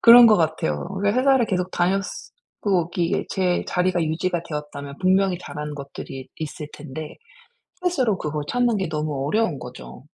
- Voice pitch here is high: No, medium, 175 Hz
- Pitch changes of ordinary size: Yes, average, 4.8 semitones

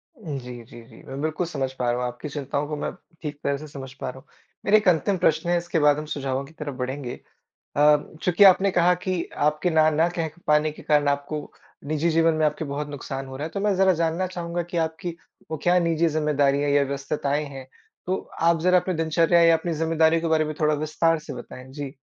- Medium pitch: Yes, medium, 155 Hz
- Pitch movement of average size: Yes, average, 3.0 semitones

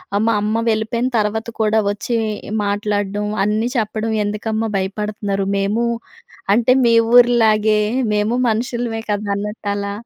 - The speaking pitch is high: Yes, high, 215 Hz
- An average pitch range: No, narrow, 1.6 semitones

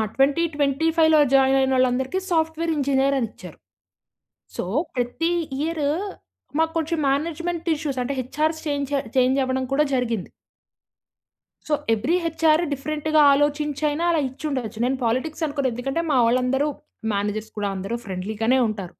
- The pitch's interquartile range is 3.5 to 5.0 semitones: Yes, average, 3.8 semitones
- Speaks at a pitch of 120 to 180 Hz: No, very high, 275 Hz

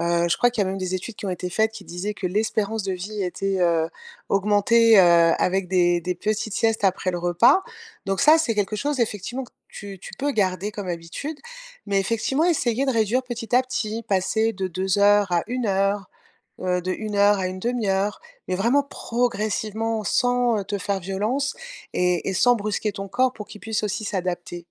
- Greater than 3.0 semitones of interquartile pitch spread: Yes, average, 3.5 semitones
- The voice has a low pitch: No, high, 205 Hz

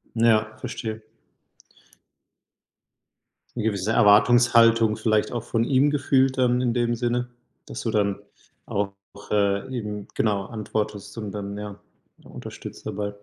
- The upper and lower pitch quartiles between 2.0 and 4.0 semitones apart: Yes, narrow, 2.6 semitones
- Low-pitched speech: Yes, low, 110 Hz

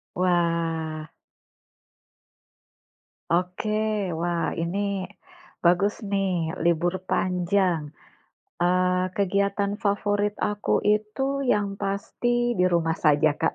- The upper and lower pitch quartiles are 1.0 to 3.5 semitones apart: Yes, average, 3.0 semitones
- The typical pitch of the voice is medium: Yes, medium, 180 Hz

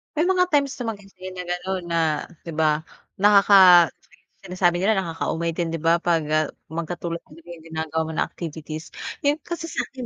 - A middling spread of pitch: Yes, average, 3.4 semitones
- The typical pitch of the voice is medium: Yes, medium, 175 Hz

